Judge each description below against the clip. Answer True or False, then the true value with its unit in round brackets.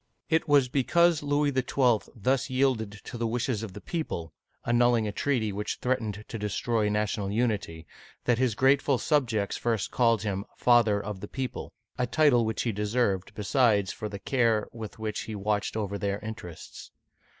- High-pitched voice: False (115 Hz)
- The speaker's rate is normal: True (180 wpm)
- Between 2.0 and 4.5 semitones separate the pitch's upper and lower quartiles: True (3.5 semitones)